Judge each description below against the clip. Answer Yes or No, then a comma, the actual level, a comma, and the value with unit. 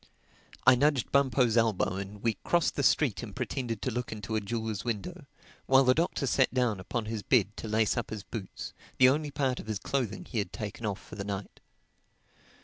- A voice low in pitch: Yes, low, 115 Hz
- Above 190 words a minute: Yes, fast, 205 wpm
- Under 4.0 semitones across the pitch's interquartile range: Yes, average, 3.6 semitones